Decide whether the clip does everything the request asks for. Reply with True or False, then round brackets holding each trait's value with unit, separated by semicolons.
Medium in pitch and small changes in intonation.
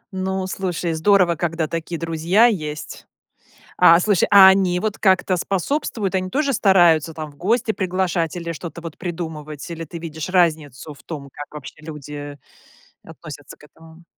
False (170 Hz; 3.2 semitones)